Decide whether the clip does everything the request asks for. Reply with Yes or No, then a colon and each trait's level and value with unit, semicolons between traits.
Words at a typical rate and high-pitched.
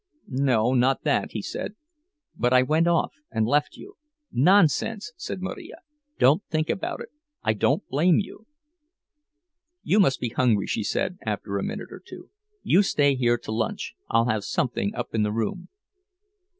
No: average, 165 wpm; low, 130 Hz